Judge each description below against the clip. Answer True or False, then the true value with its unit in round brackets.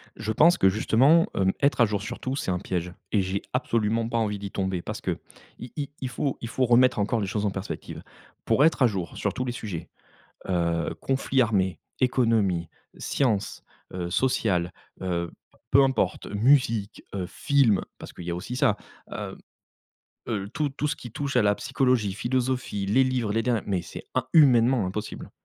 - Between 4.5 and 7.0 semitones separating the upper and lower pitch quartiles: True (4.8 semitones)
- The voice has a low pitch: True (110 Hz)